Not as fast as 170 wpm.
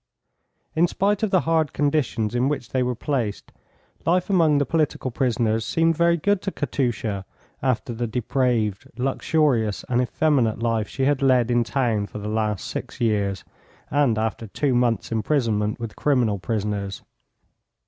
Yes: average, 155 wpm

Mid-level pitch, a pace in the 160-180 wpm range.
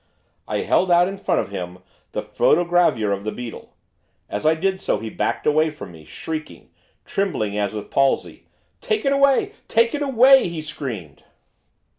Yes: medium, 155 Hz; average, 170 wpm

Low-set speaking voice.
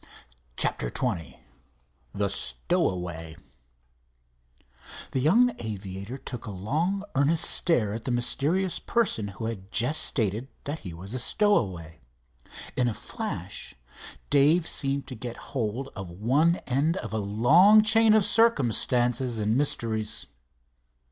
Yes: low, 120 Hz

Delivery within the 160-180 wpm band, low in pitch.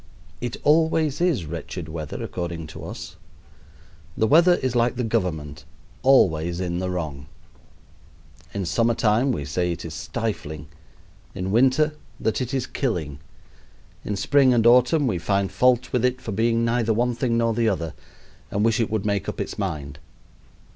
Yes: average, 165 wpm; low, 110 Hz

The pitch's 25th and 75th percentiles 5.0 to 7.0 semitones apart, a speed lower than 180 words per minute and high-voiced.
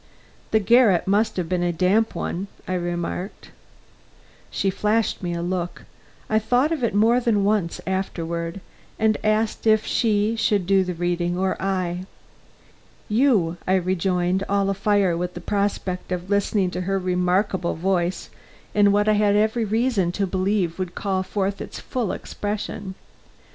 No: average, 2.7 semitones; average, 155 wpm; high, 195 Hz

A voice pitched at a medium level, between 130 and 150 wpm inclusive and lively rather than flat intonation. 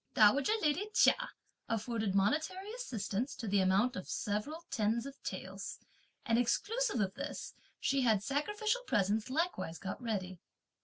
No: high, 235 Hz; average, 140 wpm; wide, 7.0 semitones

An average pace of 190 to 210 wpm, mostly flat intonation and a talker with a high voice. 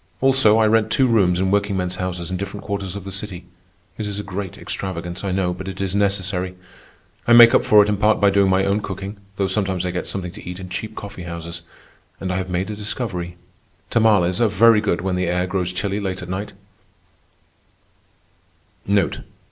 No: fast, 205 wpm; narrow, 2.2 semitones; very low, 95 Hz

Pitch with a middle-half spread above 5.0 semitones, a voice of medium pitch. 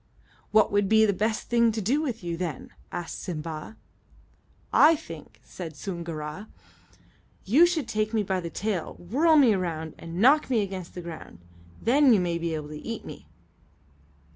No: wide, 5.4 semitones; high, 195 Hz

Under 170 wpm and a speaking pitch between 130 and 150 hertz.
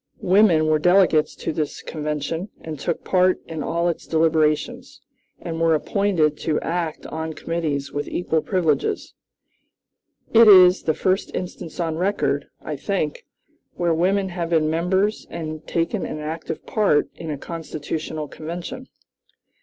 No: average, 140 wpm; medium, 165 Hz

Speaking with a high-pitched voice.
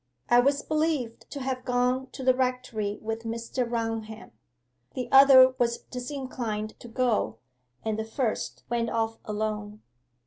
Yes: high, 240 Hz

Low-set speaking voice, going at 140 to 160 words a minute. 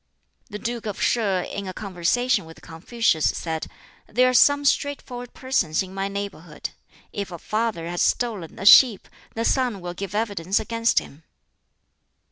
No: high, 205 Hz; average, 155 wpm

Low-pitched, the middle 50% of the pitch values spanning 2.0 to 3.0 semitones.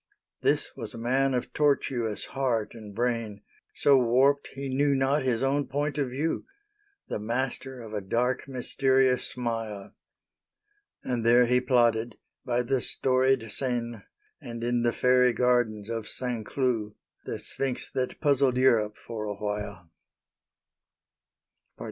Yes: low, 125 Hz; narrow, 2.6 semitones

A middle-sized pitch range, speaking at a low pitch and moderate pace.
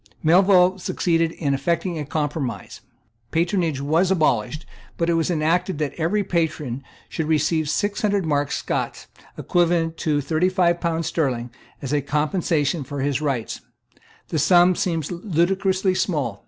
No: average, 3.3 semitones; medium, 165 Hz; average, 145 wpm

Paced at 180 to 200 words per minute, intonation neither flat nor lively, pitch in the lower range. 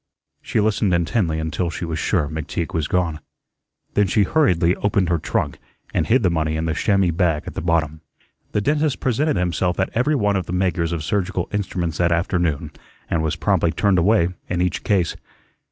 Yes: average, 190 wpm; average, 3.6 semitones; very low, 90 Hz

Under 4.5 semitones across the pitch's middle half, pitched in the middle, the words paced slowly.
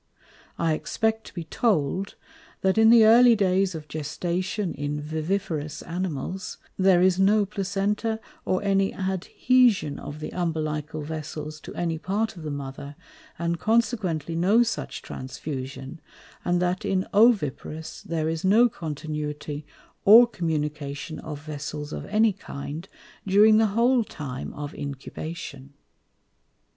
No: average, 4.9 semitones; medium, 170 Hz; slow, 130 wpm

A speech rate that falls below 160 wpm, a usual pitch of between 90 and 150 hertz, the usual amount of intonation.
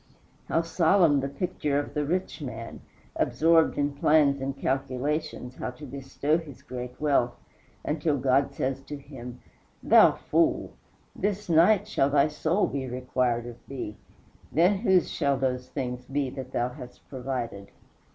Yes: average, 150 wpm; medium, 140 Hz; average, 3.5 semitones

